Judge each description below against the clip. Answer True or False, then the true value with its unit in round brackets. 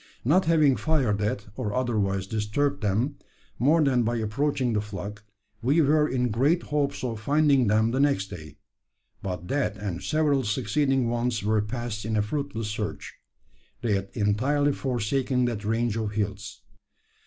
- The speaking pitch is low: True (115 Hz)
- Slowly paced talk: False (155 wpm)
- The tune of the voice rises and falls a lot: False (4.9 semitones)